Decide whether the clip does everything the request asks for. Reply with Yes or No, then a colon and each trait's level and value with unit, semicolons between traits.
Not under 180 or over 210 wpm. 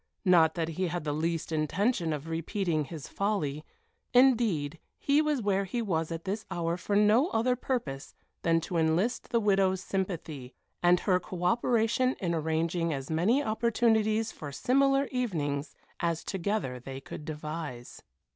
No: average, 155 wpm